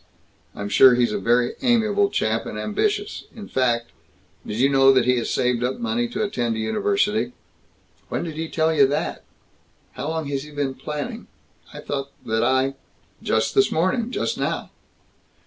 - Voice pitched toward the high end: No, medium, 140 Hz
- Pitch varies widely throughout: Yes, wide, 8.8 semitones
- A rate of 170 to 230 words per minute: Yes, average, 180 wpm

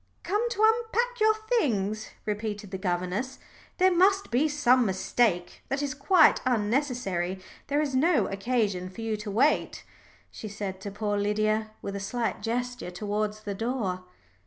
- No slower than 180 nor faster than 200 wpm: No, average, 155 wpm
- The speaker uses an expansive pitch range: Yes, wide, 6.2 semitones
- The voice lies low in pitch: No, high, 225 Hz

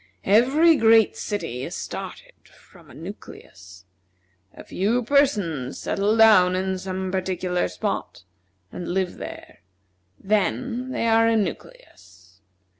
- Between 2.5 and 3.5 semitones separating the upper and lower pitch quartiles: No, average, 4.2 semitones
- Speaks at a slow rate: Yes, slow, 115 wpm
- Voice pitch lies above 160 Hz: Yes, high, 190 Hz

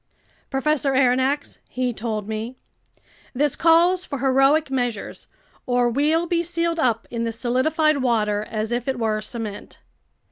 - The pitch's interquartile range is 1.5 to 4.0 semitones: No, average, 4.4 semitones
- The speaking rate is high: No, average, 140 wpm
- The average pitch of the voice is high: Yes, very high, 255 Hz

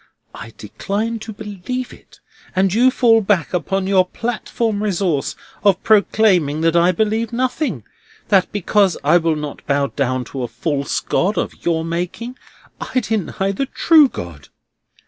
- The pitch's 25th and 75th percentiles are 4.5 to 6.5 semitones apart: Yes, average, 5.3 semitones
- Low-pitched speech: No, high, 195 Hz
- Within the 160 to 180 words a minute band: No, average, 150 wpm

